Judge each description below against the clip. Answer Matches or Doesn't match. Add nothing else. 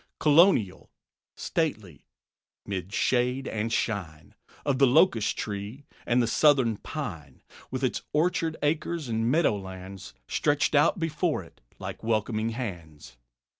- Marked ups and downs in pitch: Matches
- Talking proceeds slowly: Matches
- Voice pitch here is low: Matches